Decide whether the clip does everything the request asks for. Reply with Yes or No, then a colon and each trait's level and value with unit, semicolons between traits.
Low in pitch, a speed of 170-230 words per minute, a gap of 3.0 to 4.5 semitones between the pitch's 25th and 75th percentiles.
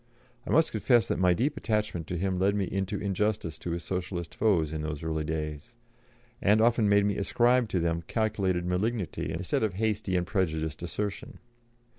Yes: very low, 95 Hz; average, 180 wpm; average, 4.1 semitones